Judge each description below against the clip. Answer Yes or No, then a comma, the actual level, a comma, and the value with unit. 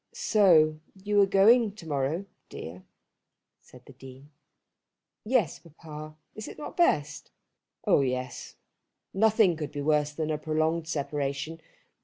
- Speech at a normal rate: No, slow, 125 wpm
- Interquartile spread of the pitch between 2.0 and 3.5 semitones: No, average, 5.2 semitones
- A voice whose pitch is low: No, medium, 155 Hz